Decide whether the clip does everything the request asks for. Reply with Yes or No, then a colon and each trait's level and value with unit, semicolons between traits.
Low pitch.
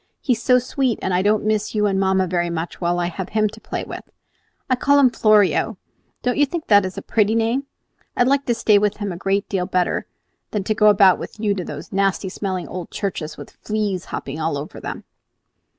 No: high, 205 Hz